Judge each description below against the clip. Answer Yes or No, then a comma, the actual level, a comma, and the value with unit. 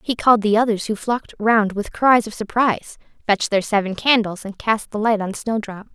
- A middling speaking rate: No, fast, 210 wpm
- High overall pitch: Yes, high, 215 Hz